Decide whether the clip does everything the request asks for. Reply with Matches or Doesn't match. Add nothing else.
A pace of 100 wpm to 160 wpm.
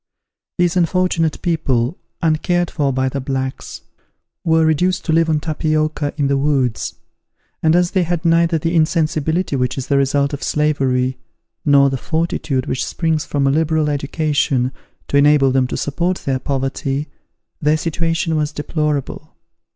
Matches